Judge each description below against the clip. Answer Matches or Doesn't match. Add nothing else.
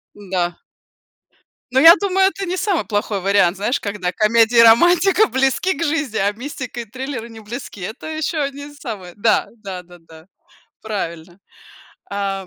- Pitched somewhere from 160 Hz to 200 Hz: Doesn't match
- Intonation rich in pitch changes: Matches